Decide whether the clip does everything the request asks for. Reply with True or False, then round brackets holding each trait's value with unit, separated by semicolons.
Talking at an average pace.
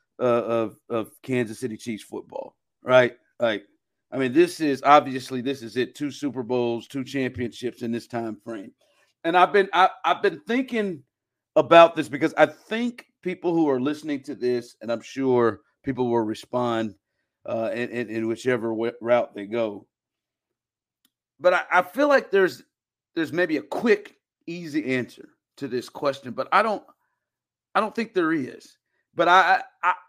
True (170 wpm)